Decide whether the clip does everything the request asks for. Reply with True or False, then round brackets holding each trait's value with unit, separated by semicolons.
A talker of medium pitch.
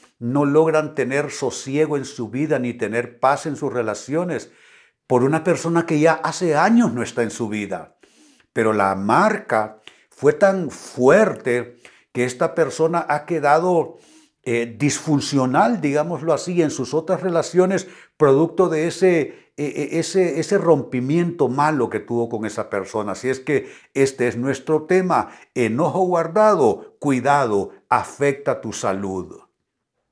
True (145 Hz)